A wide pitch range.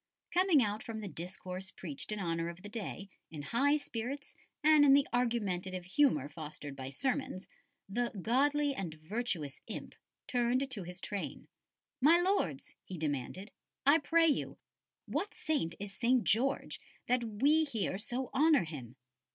Yes: wide, 7.5 semitones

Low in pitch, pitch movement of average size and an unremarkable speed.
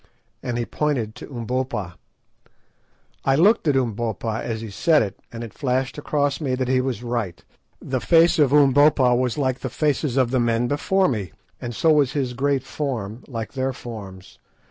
Yes: low, 130 Hz; average, 3.5 semitones; average, 180 wpm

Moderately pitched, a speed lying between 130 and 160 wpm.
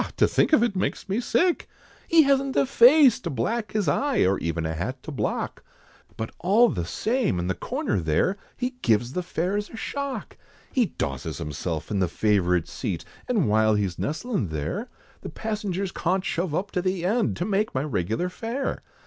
No: medium, 180 Hz; average, 190 wpm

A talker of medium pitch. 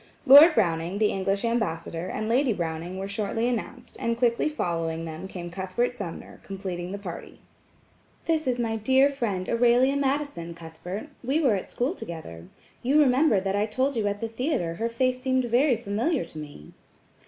No: high, 220 Hz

